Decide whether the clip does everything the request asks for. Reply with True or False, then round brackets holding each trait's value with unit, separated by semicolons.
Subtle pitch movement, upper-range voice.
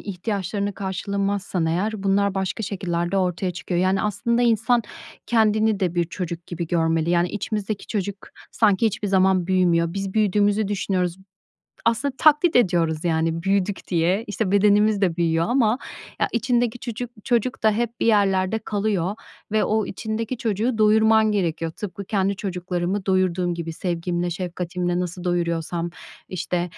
False (3.5 semitones; 195 Hz)